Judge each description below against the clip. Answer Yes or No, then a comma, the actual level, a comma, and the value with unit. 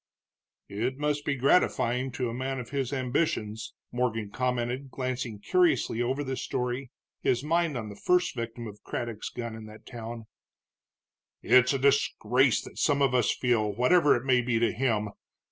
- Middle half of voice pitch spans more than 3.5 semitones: No, average, 2.7 semitones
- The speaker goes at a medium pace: Yes, average, 165 wpm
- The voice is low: Yes, low, 125 Hz